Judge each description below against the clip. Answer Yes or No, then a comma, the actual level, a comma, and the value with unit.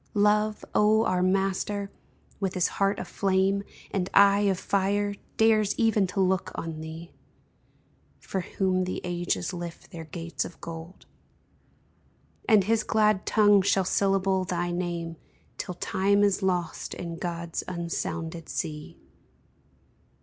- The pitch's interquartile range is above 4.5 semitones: No, average, 2.7 semitones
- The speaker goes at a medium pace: No, slow, 130 wpm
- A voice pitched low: No, high, 190 Hz